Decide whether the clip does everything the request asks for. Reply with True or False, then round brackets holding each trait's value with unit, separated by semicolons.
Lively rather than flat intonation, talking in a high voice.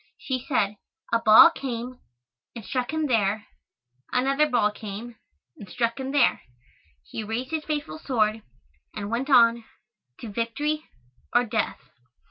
False (3.7 semitones; 240 Hz)